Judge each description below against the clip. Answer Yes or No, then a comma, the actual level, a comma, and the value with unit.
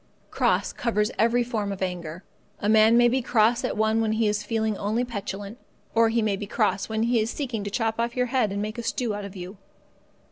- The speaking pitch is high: Yes, high, 220 Hz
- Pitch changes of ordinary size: No, narrow, 2.2 semitones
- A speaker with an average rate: No, fast, 235 wpm